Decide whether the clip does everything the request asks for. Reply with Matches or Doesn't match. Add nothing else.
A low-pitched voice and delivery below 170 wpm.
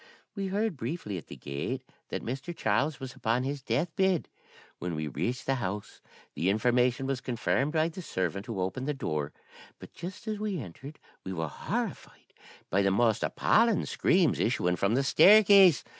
Doesn't match